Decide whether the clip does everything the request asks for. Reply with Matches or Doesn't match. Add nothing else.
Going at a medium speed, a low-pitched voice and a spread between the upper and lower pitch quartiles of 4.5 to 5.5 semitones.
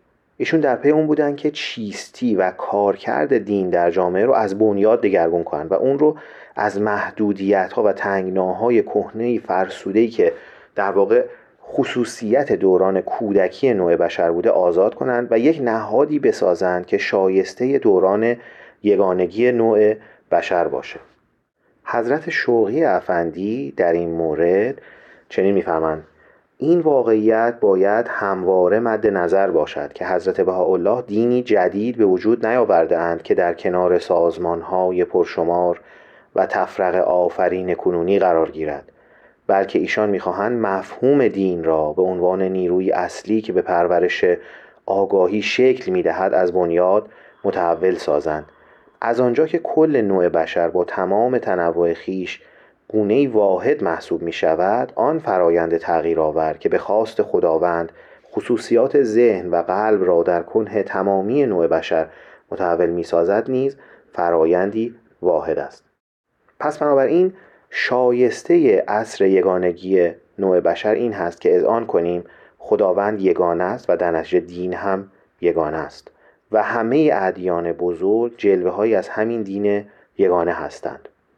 Matches